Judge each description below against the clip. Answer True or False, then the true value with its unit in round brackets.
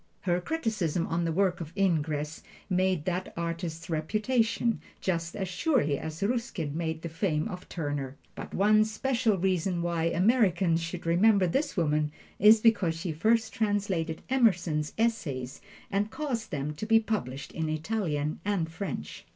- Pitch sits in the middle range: True (180 Hz)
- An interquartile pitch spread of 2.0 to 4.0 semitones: False (4.9 semitones)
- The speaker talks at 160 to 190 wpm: False (150 wpm)